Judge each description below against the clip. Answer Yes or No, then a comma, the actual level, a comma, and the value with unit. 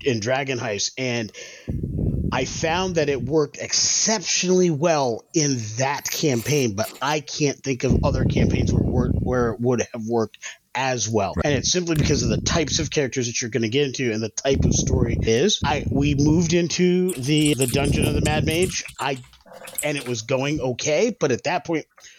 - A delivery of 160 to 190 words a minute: No, average, 200 wpm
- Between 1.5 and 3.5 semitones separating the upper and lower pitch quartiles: No, average, 4.3 semitones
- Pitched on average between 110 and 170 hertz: Yes, medium, 140 Hz